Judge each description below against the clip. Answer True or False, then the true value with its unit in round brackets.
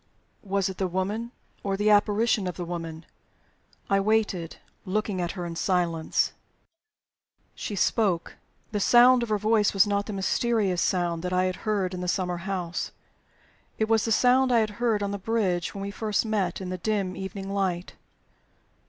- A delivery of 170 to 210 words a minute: True (180 wpm)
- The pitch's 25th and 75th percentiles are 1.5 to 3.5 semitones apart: True (2.9 semitones)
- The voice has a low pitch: False (195 Hz)